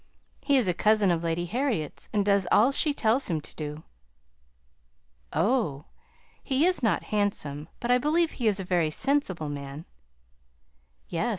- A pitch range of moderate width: No, wide, 7.7 semitones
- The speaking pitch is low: No, high, 200 Hz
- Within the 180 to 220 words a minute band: No, average, 160 wpm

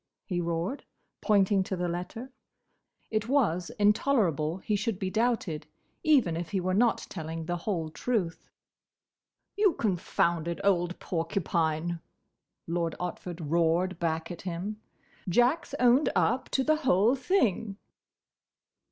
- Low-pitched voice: No, medium, 185 Hz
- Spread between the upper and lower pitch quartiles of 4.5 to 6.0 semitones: Yes, average, 5.0 semitones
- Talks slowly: Yes, slow, 125 wpm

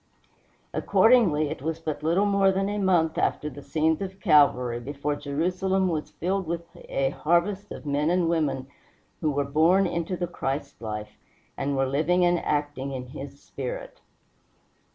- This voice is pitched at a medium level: Yes, medium, 155 Hz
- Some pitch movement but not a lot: Yes, average, 4.3 semitones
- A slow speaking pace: No, average, 160 wpm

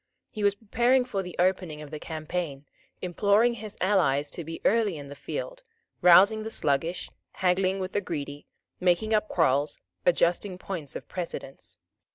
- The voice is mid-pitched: Yes, medium, 180 Hz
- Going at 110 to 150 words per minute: No, average, 160 wpm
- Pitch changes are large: No, average, 4.8 semitones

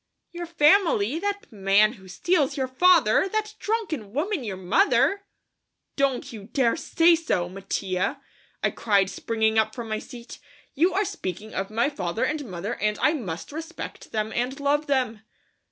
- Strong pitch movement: Yes, wide, 7.8 semitones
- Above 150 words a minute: Yes, average, 160 wpm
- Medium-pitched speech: No, very high, 250 Hz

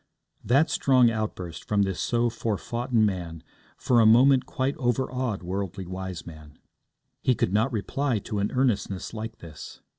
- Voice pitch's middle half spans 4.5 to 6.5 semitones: Yes, average, 4.9 semitones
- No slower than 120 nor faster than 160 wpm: Yes, average, 145 wpm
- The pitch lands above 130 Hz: No, low, 110 Hz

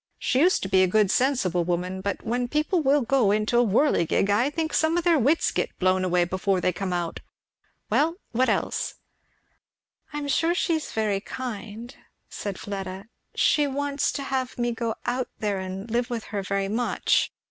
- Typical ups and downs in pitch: No, wide, 6.1 semitones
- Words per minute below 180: No, average, 190 wpm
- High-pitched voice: Yes, high, 230 Hz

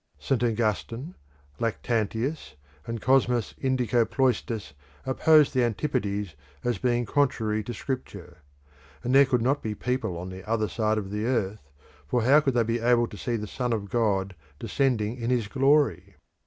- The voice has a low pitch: Yes, low, 115 Hz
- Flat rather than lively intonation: No, average, 3.4 semitones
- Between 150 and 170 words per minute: Yes, average, 155 wpm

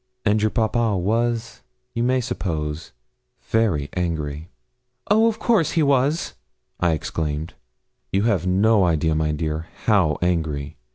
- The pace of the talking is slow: Yes, slow, 125 wpm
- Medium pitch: No, very low, 95 Hz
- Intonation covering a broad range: Yes, wide, 6.9 semitones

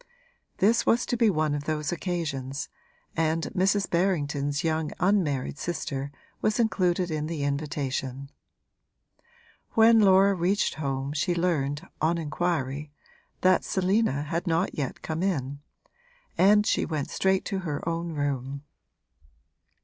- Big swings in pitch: No, average, 4.5 semitones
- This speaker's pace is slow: Yes, slow, 125 wpm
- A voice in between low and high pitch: Yes, medium, 160 Hz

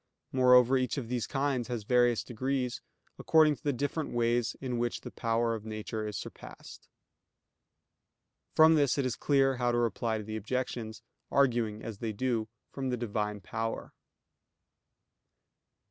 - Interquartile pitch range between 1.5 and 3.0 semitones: Yes, average, 2.7 semitones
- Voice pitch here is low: Yes, low, 120 Hz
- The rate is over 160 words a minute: No, average, 145 wpm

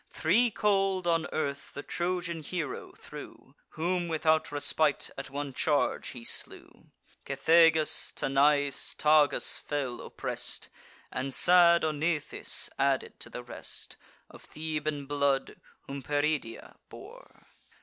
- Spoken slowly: Yes, slow, 115 wpm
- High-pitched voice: No, medium, 155 Hz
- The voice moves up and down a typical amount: Yes, average, 3.1 semitones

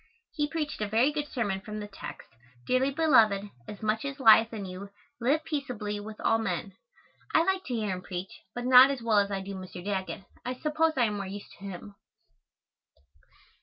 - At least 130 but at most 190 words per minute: No, average, 200 wpm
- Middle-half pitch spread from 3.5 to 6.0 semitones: Yes, average, 5.1 semitones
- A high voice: Yes, high, 220 Hz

